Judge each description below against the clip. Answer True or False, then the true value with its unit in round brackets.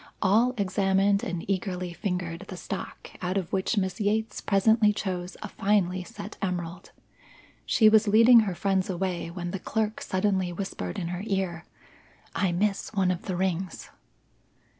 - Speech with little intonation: True (2.3 semitones)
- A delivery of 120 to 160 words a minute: True (155 wpm)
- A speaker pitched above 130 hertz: True (190 Hz)